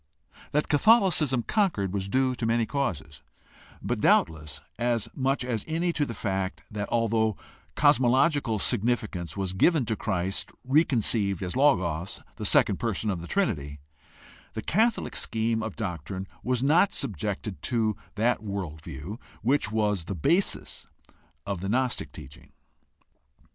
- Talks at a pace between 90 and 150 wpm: Yes, average, 140 wpm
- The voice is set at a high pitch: No, low, 110 Hz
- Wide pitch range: Yes, wide, 5.7 semitones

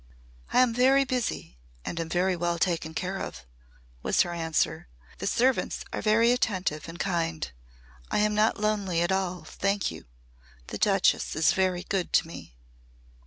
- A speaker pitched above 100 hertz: Yes, medium, 185 Hz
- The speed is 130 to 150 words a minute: No, average, 165 wpm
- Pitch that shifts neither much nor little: Yes, average, 4.1 semitones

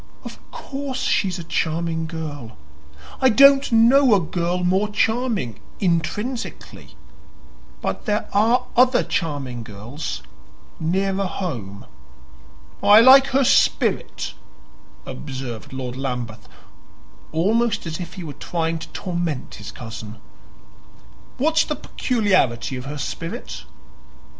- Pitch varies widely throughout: Yes, wide, 8.9 semitones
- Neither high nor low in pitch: Yes, medium, 175 Hz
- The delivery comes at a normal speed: No, slow, 110 wpm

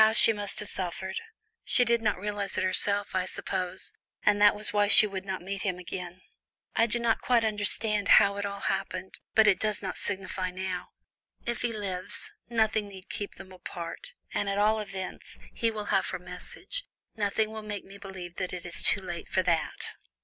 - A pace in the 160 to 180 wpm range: No, average, 200 wpm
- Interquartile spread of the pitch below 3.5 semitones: Yes, narrow, 2.4 semitones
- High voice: Yes, high, 200 Hz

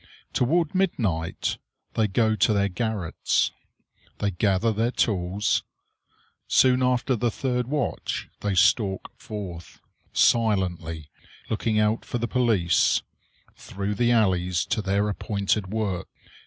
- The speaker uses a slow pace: Yes, slow, 115 wpm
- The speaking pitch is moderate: No, low, 105 Hz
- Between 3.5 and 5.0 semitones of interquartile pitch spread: Yes, average, 3.9 semitones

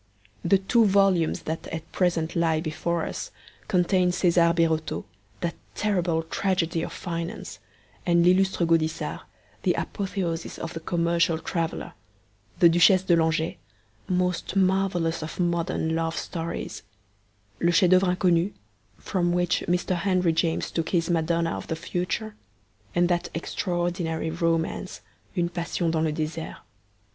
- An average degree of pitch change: No, narrow, 1.8 semitones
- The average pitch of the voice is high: No, medium, 170 Hz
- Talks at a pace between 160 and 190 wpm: No, slow, 135 wpm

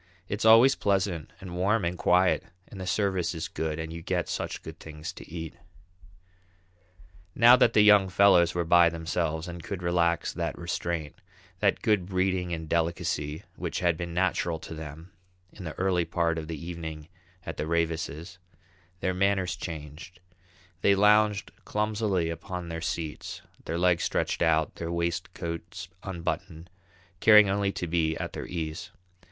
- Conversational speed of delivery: Yes, average, 160 wpm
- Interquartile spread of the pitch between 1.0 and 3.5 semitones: Yes, narrow, 2.4 semitones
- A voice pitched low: Yes, very low, 85 Hz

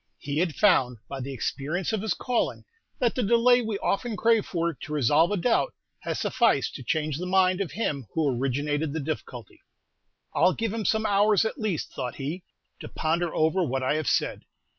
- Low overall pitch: No, medium, 170 Hz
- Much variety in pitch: Yes, wide, 6.9 semitones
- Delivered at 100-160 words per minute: No, average, 195 wpm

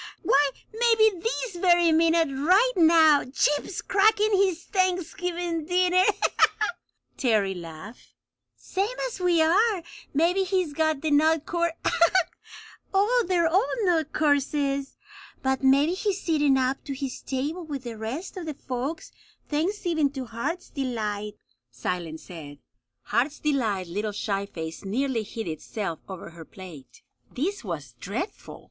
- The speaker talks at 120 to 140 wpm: Yes, slow, 135 wpm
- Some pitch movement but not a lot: No, wide, 7.7 semitones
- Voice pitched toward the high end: Yes, very high, 300 Hz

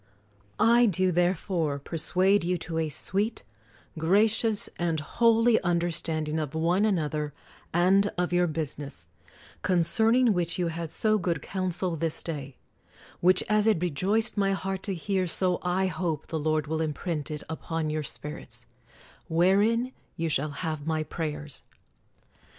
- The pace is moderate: Yes, average, 150 wpm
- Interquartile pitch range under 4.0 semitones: Yes, average, 3.6 semitones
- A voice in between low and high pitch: Yes, medium, 175 Hz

